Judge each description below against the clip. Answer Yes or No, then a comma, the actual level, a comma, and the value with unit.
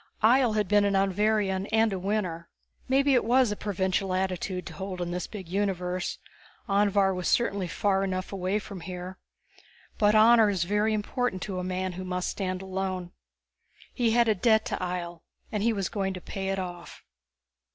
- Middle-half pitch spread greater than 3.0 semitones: No, narrow, 2.4 semitones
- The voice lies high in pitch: Yes, high, 195 Hz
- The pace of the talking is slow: No, average, 185 wpm